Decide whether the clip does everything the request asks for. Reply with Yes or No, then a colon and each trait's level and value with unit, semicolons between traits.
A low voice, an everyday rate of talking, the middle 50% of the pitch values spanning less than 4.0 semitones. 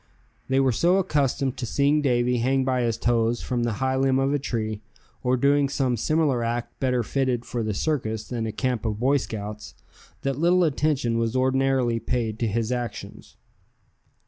Yes: low, 125 Hz; average, 180 wpm; average, 2.8 semitones